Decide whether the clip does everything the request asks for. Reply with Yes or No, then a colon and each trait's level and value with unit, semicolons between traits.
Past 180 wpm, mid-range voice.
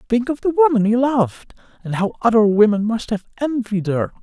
No: average, 200 wpm; high, 230 Hz